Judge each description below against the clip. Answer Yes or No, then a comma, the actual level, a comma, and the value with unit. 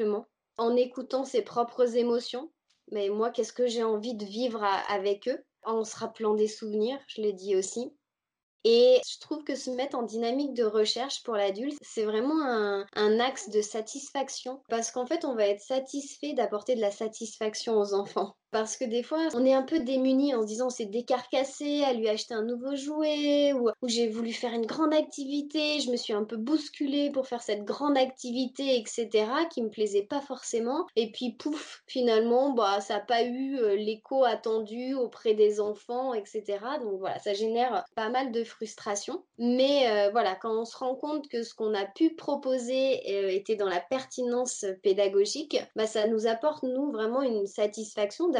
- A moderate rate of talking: Yes, average, 190 wpm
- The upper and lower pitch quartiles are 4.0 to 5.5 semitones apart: No, average, 3.6 semitones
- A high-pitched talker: Yes, high, 240 Hz